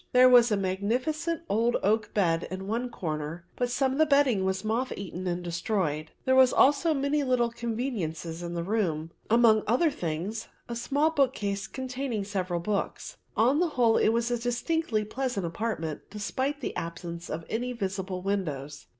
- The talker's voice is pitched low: No, high, 220 Hz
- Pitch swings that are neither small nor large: No, wide, 5.7 semitones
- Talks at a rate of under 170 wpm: No, average, 175 wpm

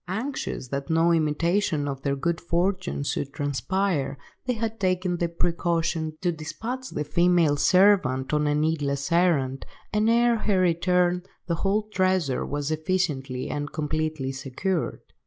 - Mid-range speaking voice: Yes, medium, 170 Hz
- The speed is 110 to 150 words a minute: Yes, average, 140 wpm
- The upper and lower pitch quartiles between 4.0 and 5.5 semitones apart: Yes, average, 4.3 semitones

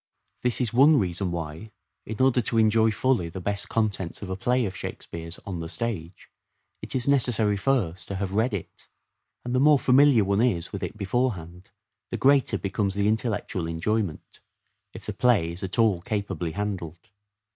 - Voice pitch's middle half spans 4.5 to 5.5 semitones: Yes, average, 4.8 semitones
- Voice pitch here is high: No, low, 105 Hz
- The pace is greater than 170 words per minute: Yes, average, 180 wpm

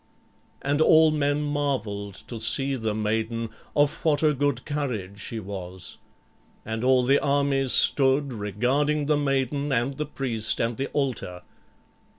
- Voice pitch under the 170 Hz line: Yes, low, 135 Hz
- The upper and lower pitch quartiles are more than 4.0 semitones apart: Yes, average, 4.5 semitones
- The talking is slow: No, average, 145 wpm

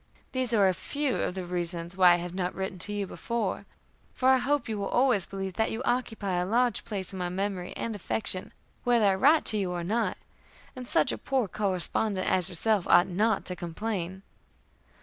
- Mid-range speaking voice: No, high, 195 Hz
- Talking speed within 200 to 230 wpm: Yes, fast, 205 wpm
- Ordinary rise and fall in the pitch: Yes, average, 4.0 semitones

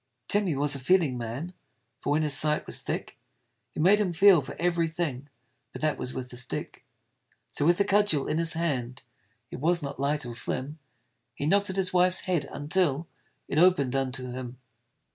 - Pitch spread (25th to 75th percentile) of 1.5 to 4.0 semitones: No, average, 4.8 semitones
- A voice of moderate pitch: Yes, medium, 150 Hz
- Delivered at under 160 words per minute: No, average, 195 wpm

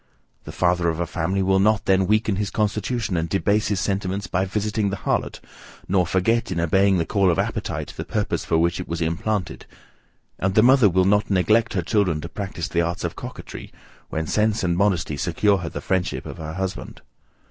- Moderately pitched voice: No, very low, 95 Hz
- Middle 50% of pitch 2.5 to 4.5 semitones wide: Yes, average, 3.1 semitones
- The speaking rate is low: No, average, 200 wpm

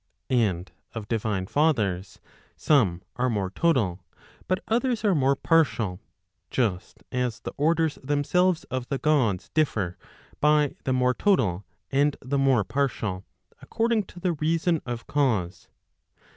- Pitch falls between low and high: No, low, 130 Hz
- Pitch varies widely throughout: Yes, wide, 7.0 semitones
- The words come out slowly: Yes, slow, 130 wpm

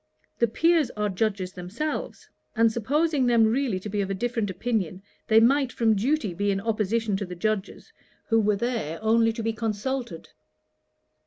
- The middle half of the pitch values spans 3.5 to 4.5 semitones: No, average, 3.1 semitones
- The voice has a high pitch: Yes, high, 220 Hz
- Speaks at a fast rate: No, average, 170 wpm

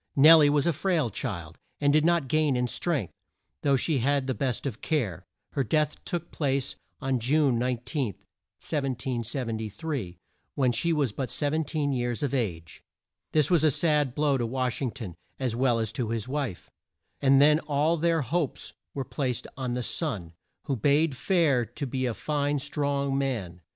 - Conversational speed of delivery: Yes, average, 170 wpm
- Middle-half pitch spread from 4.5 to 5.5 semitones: No, average, 3.7 semitones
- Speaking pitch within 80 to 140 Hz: Yes, low, 135 Hz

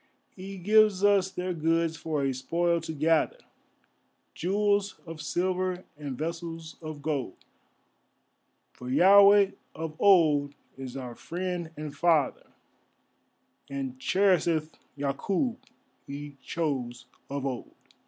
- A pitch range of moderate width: Yes, average, 4.6 semitones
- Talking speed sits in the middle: No, slow, 110 wpm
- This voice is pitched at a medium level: Yes, medium, 165 Hz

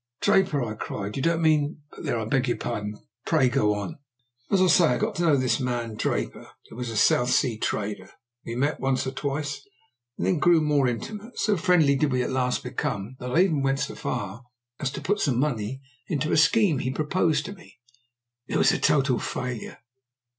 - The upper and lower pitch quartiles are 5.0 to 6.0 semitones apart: No, average, 4.3 semitones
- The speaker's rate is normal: No, fast, 210 wpm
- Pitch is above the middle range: No, low, 135 Hz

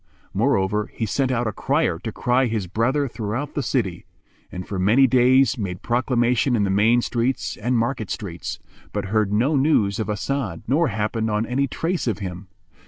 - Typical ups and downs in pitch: Yes, average, 4.3 semitones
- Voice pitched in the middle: No, low, 115 Hz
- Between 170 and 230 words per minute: Yes, average, 180 wpm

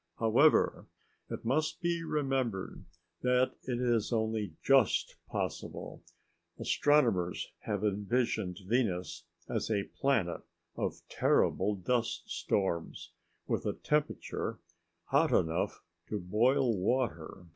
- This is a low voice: Yes, low, 115 Hz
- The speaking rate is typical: No, slow, 105 wpm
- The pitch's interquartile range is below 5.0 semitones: No, average, 5.3 semitones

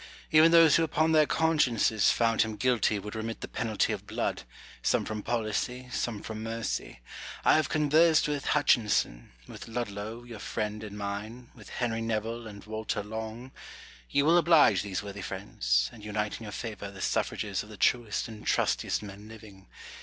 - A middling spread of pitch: Yes, average, 3.1 semitones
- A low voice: Yes, low, 110 Hz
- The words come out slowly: No, average, 175 wpm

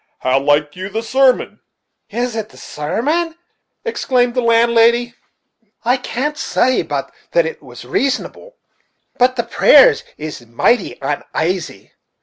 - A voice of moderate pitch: No, high, 235 Hz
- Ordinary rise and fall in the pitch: No, wide, 5.9 semitones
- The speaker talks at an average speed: No, slow, 125 wpm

